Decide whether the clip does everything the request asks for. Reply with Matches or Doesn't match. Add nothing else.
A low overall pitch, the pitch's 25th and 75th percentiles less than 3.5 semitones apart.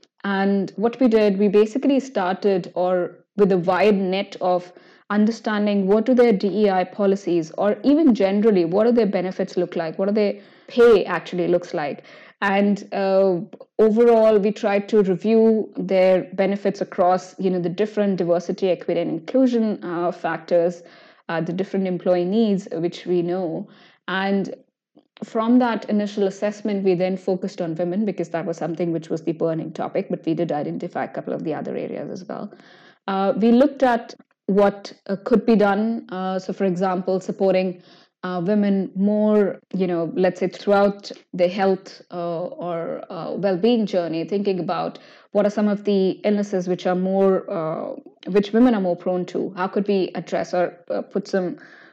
Doesn't match